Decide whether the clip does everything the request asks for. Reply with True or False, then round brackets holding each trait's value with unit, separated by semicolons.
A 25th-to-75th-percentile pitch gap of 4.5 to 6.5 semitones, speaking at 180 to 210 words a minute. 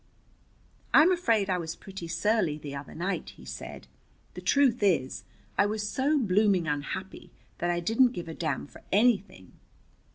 False (5.2 semitones; 160 wpm)